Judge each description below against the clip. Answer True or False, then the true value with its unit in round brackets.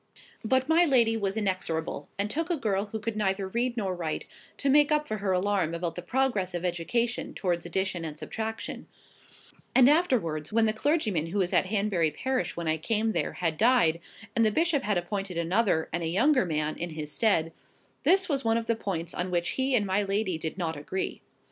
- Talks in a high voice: True (200 Hz)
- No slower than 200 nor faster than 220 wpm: True (205 wpm)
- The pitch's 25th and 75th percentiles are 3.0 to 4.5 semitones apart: False (5.2 semitones)